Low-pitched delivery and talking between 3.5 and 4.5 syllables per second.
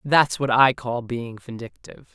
Yes: low, 125 Hz; 4.4 syllables/s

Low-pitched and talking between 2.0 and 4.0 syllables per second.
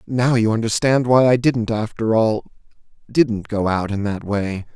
No: low, 115 Hz; 4.3 syllables/s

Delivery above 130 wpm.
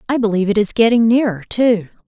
Yes: fast, 205 wpm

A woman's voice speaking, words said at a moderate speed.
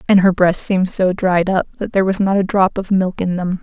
No: female; fast, 280 wpm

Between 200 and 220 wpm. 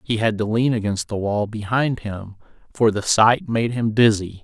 Yes: fast, 205 wpm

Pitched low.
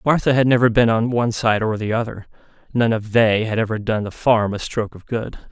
Yes: low, 115 Hz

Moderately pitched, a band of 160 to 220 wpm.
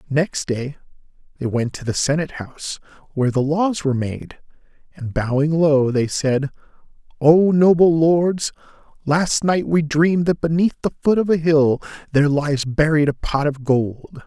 Yes: medium, 150 Hz; average, 165 wpm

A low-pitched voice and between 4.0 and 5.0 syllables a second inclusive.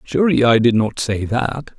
Yes: low, 120 Hz; 4.8 syllables/s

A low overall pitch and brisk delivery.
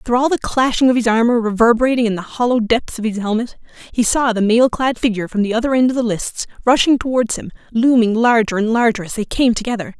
No: high, 230 Hz; fast, 235 wpm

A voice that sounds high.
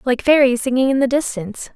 Yes: very high, 255 Hz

